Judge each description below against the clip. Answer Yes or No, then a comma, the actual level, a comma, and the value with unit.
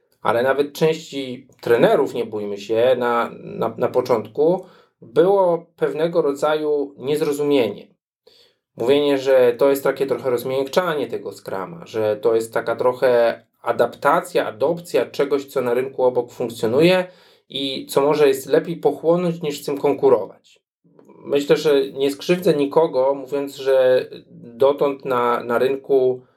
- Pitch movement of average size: No, wide, 6.3 semitones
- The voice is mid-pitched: Yes, medium, 145 Hz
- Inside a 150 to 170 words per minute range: No, average, 130 wpm